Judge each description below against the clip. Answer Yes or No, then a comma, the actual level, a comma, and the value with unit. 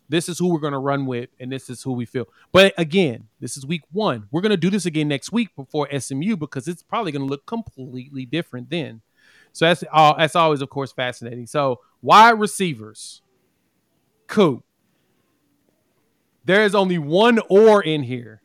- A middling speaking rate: Yes, average, 190 wpm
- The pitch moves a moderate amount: No, wide, 5.7 semitones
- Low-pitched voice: No, medium, 155 Hz